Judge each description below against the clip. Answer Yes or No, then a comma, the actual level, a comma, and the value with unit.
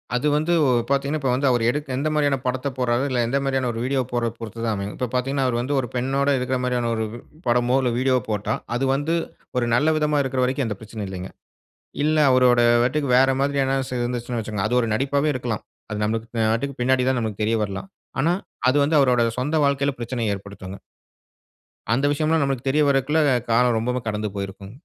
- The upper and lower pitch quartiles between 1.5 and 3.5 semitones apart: Yes, average, 3.2 semitones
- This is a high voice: No, low, 125 Hz